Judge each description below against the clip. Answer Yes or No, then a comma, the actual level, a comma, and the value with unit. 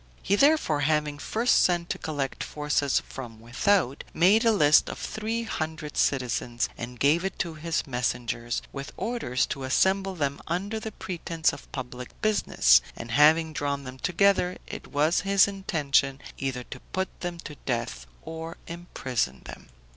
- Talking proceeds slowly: No, average, 155 wpm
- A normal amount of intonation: No, wide, 5.9 semitones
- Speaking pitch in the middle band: Yes, medium, 155 Hz